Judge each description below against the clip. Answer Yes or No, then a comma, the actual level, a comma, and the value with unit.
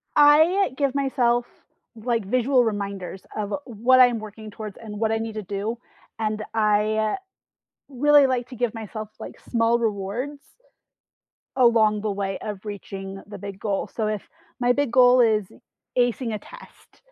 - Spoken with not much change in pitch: No, average, 3.0 semitones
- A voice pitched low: No, high, 225 Hz